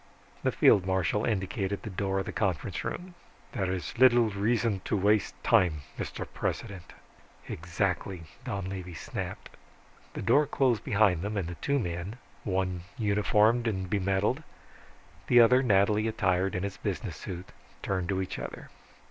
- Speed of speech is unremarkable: Yes, average, 150 wpm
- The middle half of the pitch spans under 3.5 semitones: Yes, average, 2.9 semitones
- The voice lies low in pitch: Yes, low, 100 Hz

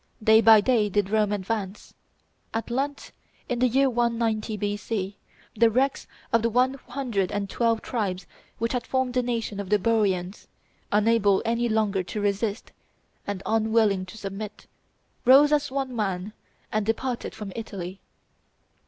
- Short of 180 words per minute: Yes, average, 150 wpm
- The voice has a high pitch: Yes, high, 220 Hz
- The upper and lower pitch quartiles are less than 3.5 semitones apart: Yes, average, 2.8 semitones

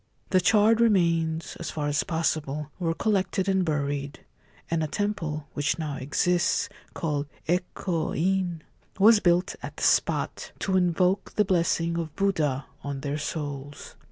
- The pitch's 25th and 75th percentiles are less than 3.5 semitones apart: No, average, 3.9 semitones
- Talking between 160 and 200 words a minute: No, average, 150 wpm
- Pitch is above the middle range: No, medium, 165 Hz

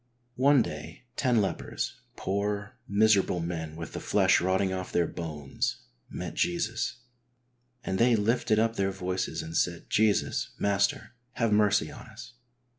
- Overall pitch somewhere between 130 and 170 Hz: No, low, 100 Hz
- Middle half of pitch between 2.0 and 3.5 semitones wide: No, average, 4.0 semitones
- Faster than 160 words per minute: No, average, 140 wpm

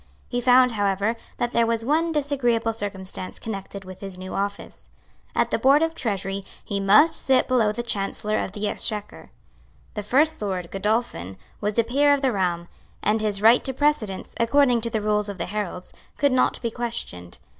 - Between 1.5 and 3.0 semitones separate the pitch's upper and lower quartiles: No, average, 4.0 semitones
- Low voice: No, high, 215 Hz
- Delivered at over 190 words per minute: No, average, 185 wpm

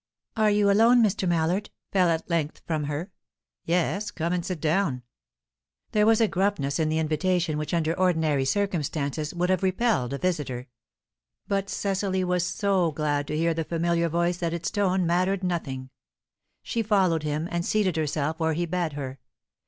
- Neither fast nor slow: Yes, average, 170 wpm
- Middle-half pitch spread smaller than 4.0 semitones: Yes, average, 3.5 semitones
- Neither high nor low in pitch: Yes, medium, 170 Hz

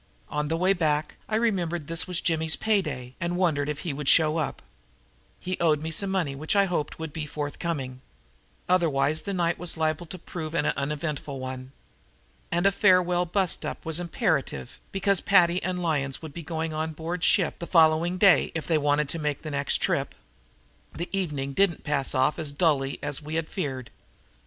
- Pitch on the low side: No, medium, 160 Hz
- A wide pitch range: No, average, 3.1 semitones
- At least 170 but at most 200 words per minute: Yes, average, 195 wpm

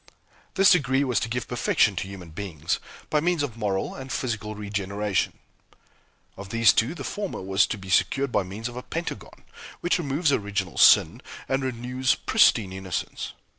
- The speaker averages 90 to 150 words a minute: No, average, 170 wpm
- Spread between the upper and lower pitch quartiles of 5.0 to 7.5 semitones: Yes, average, 5.3 semitones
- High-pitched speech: No, low, 115 Hz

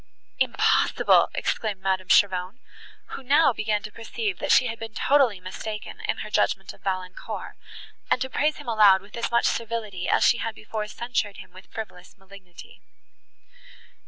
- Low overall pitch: No, high, 215 Hz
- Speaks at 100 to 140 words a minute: No, average, 160 wpm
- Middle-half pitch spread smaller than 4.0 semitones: Yes, average, 3.5 semitones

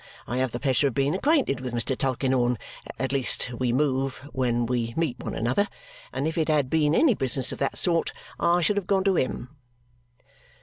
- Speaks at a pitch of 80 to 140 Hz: Yes, low, 135 Hz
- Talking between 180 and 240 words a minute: Yes, average, 200 wpm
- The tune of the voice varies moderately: Yes, average, 4.3 semitones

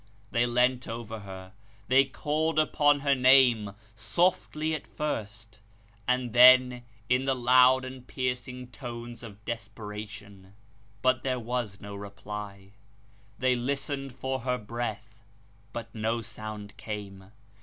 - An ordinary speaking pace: No, slow, 125 wpm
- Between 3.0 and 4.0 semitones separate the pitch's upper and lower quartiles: Yes, average, 3.4 semitones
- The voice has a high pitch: No, low, 120 Hz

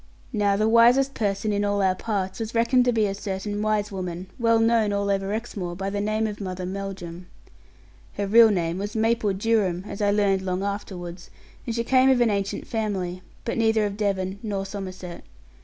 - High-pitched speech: Yes, high, 205 Hz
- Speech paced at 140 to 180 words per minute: No, average, 195 wpm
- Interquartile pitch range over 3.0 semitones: No, narrow, 2.5 semitones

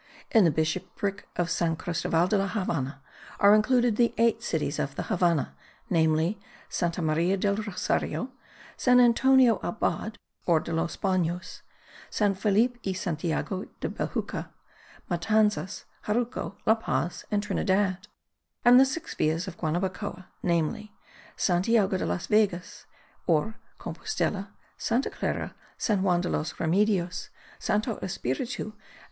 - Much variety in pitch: No, average, 4.1 semitones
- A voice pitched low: No, high, 195 Hz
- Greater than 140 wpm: No, slow, 135 wpm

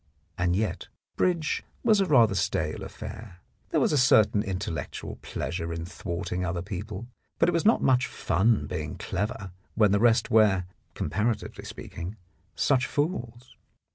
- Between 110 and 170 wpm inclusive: Yes, average, 145 wpm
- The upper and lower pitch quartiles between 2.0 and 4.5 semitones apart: No, average, 5.3 semitones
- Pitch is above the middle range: No, low, 105 Hz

